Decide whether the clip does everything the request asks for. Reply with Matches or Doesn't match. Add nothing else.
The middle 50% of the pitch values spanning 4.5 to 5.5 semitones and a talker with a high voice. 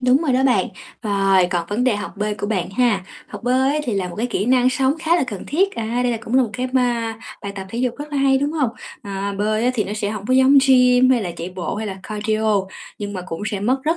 Doesn't match